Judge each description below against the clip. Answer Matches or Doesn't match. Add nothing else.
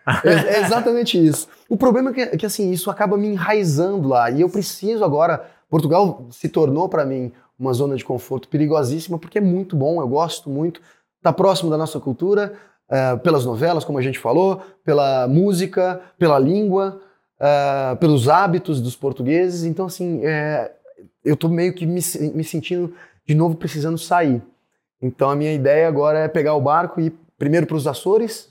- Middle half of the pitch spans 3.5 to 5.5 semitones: Matches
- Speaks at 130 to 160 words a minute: Doesn't match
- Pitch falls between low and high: Matches